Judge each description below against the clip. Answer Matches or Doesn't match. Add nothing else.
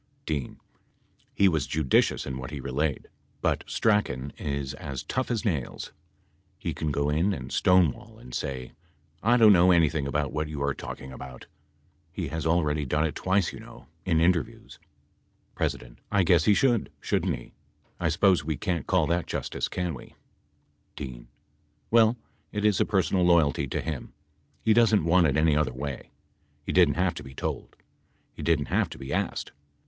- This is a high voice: Doesn't match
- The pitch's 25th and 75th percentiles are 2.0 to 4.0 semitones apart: Doesn't match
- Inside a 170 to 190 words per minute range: Matches